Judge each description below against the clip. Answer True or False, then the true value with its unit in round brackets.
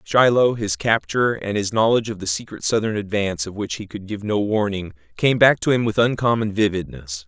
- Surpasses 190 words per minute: True (205 wpm)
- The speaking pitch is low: True (105 Hz)